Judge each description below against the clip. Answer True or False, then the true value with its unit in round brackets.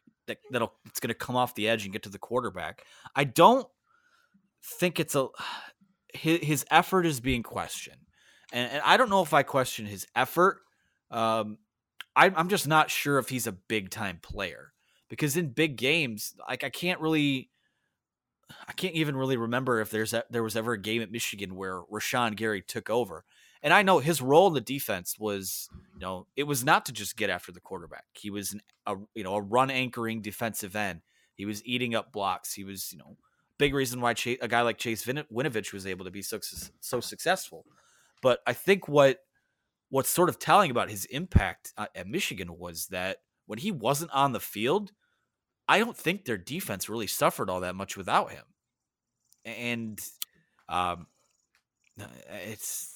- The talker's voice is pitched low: True (120 Hz)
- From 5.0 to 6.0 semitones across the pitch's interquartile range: True (5.4 semitones)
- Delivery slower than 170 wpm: False (185 wpm)